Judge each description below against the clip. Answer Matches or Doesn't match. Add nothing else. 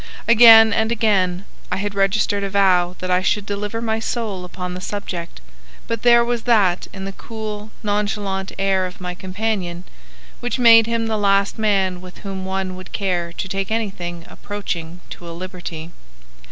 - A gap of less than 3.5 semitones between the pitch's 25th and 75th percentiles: Matches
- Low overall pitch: Doesn't match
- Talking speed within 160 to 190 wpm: Matches